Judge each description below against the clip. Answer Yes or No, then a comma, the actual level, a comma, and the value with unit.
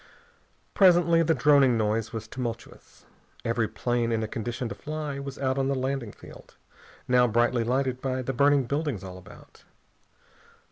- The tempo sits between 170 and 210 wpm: No, average, 155 wpm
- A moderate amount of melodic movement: Yes, average, 3.2 semitones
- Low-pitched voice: Yes, low, 130 Hz